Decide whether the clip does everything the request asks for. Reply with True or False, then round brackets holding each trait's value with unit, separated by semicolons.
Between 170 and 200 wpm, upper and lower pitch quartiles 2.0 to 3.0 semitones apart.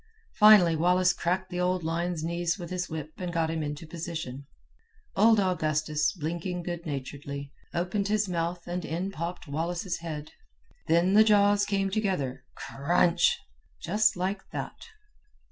False (145 wpm; 2.7 semitones)